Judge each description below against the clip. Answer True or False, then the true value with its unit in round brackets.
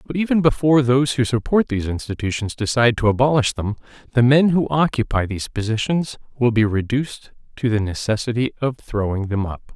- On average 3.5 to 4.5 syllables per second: False (5.9 syllables/s)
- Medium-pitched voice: False (120 Hz)